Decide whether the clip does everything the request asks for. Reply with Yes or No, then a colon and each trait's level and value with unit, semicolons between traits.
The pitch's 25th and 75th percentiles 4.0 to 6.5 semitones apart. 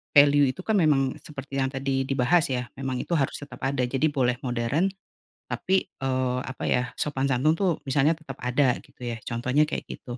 No: average, 2.8 semitones